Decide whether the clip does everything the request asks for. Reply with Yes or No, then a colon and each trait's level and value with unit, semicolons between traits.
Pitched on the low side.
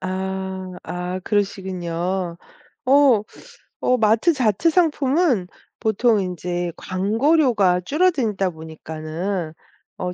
No: high, 190 Hz